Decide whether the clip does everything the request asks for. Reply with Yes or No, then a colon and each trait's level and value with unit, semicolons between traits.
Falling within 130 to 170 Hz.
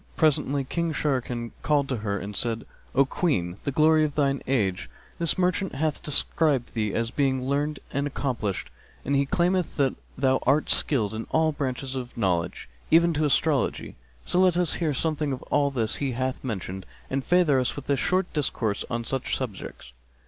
Yes: medium, 140 Hz